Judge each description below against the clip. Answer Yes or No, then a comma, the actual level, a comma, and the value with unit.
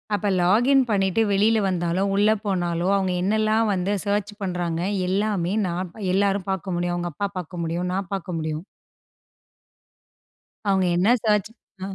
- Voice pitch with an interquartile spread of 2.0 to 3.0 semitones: Yes, narrow, 2.5 semitones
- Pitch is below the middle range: No, high, 190 Hz